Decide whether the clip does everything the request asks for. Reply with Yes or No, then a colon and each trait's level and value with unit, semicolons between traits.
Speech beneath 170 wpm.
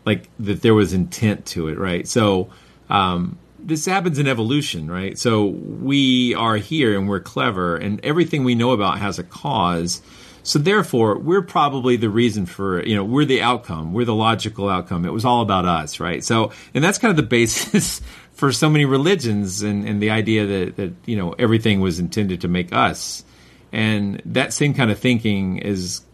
No: average, 195 wpm